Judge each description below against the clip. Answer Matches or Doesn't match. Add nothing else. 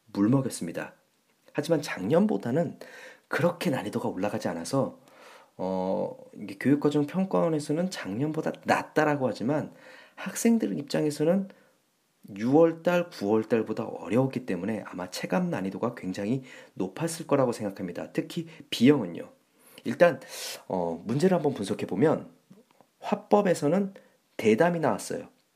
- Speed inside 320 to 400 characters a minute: Doesn't match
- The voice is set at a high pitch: Doesn't match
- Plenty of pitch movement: Matches